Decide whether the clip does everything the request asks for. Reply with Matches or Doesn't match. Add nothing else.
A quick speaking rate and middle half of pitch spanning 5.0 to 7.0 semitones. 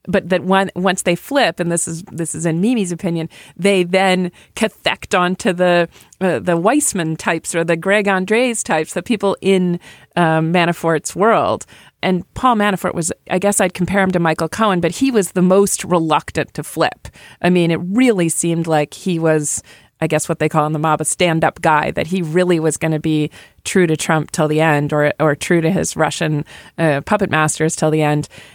Doesn't match